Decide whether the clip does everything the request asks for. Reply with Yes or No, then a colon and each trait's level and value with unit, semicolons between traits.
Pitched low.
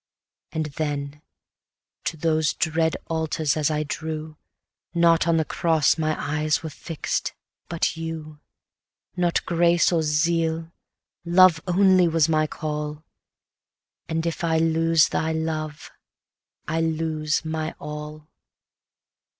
No: medium, 160 Hz